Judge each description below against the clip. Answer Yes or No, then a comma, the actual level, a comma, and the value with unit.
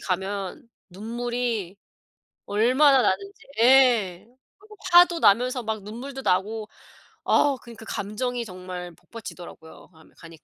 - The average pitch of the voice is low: No, high, 225 Hz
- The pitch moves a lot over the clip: No, average, 4.9 semitones